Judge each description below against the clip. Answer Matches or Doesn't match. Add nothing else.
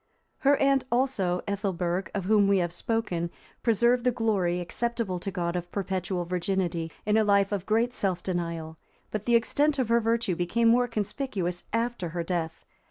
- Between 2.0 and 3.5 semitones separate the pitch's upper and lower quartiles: Doesn't match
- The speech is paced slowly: Doesn't match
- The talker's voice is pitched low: Doesn't match